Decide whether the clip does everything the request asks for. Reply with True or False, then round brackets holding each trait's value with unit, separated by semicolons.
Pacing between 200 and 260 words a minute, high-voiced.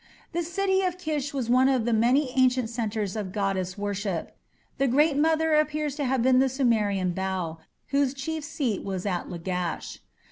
False (175 wpm; 255 Hz)